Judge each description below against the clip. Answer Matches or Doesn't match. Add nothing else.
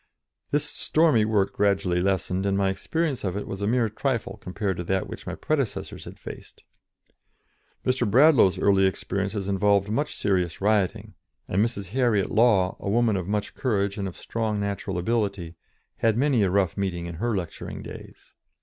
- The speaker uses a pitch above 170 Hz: Doesn't match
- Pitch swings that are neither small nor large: Matches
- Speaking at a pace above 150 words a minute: Matches